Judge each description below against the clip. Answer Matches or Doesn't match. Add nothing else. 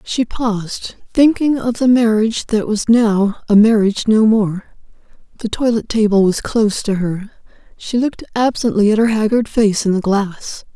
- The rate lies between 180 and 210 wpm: Doesn't match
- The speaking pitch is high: Matches